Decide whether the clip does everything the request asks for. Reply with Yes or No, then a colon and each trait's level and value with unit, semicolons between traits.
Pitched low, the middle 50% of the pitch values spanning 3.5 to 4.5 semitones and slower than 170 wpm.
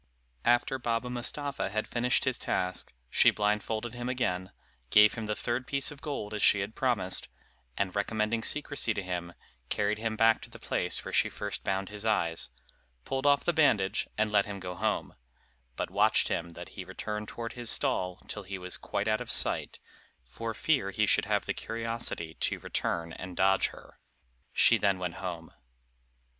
No: low, 105 Hz; average, 3.9 semitones; average, 180 wpm